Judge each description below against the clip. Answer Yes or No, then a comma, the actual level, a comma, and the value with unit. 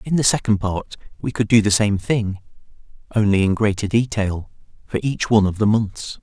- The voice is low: Yes, low, 105 Hz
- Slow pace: No, average, 195 wpm